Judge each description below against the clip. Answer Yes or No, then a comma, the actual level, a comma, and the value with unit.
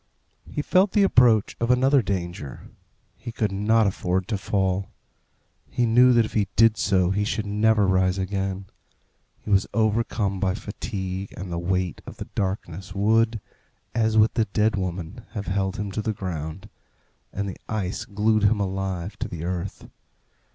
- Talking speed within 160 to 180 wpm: Yes, average, 165 wpm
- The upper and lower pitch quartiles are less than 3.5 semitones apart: Yes, average, 2.9 semitones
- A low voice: Yes, low, 100 Hz